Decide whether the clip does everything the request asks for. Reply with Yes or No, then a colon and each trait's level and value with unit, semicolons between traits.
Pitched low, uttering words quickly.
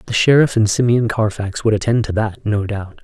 Yes: low, 110 Hz; fast, 220 wpm